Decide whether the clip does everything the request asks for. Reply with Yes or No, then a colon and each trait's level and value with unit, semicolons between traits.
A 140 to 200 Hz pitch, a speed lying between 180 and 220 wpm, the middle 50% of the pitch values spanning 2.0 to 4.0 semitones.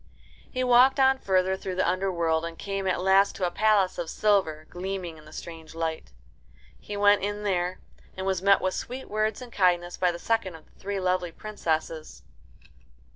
Yes: high, 190 Hz; average, 185 wpm; average, 2.9 semitones